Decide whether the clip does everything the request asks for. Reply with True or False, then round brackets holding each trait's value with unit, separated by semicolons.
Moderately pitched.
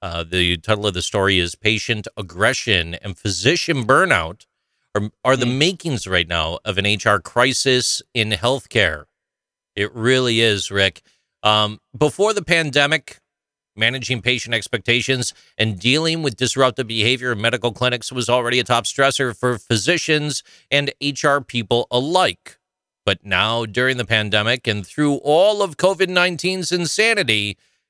False (120 Hz)